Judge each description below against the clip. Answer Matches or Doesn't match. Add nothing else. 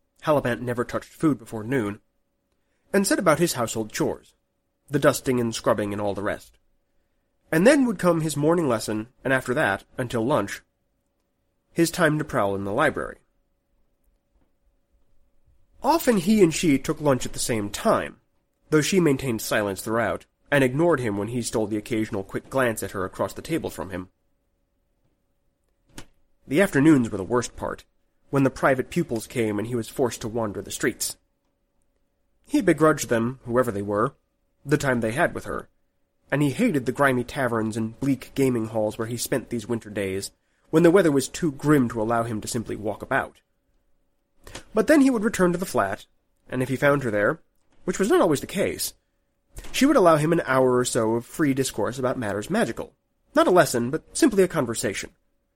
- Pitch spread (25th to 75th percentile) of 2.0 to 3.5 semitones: Doesn't match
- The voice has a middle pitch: Doesn't match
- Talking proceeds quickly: Doesn't match